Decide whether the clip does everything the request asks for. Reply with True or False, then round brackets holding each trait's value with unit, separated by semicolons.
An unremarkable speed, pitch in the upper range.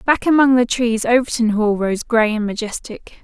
True (185 wpm; 230 Hz)